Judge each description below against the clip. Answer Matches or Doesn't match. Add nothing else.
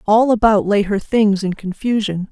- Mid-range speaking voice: Doesn't match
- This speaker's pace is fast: Doesn't match